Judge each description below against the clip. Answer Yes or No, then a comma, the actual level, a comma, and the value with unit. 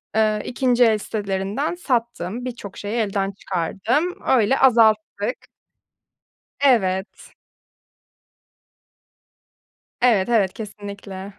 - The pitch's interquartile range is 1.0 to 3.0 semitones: No, average, 3.5 semitones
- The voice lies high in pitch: Yes, high, 215 Hz